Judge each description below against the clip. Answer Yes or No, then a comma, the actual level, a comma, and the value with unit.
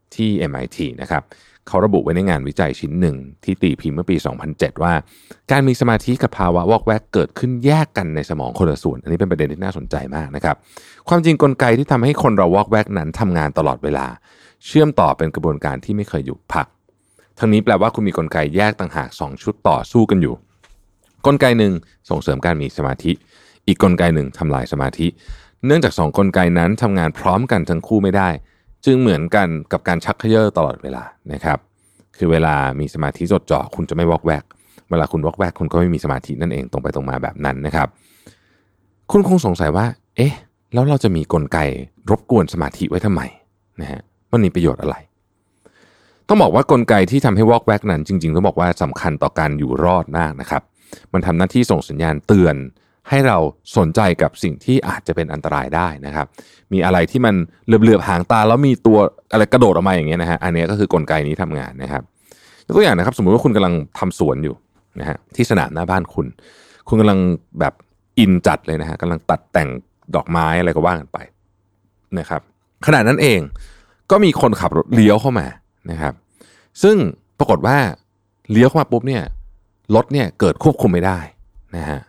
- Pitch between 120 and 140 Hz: No, very low, 90 Hz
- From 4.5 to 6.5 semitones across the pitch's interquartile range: Yes, average, 5.1 semitones